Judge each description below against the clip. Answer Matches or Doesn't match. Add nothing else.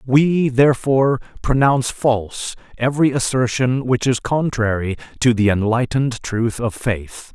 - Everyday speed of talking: Doesn't match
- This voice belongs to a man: Matches